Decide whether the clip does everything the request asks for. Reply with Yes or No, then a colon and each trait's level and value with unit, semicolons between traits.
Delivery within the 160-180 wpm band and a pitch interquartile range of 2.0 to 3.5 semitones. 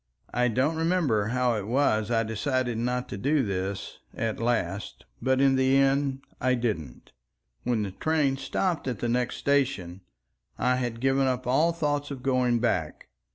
Yes: average, 165 wpm; average, 3.2 semitones